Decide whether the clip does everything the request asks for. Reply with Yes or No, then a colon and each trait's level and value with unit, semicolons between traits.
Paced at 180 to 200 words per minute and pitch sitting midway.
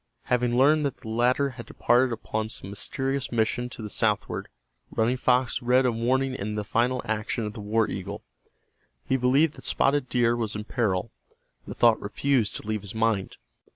No: average, 185 wpm; low, 120 Hz